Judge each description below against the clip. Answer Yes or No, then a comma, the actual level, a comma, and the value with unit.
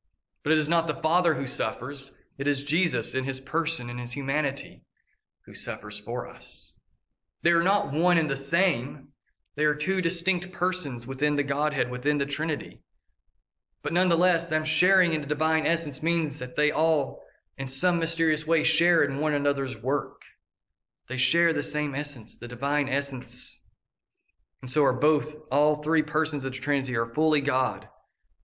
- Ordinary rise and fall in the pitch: Yes, average, 3.3 semitones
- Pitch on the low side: No, medium, 150 Hz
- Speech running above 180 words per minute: No, average, 170 wpm